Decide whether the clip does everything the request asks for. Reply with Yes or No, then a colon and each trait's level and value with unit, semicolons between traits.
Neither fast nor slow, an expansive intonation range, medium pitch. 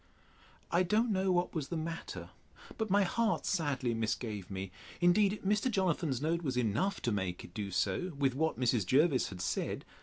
Yes: average, 180 wpm; wide, 8.4 semitones; medium, 155 Hz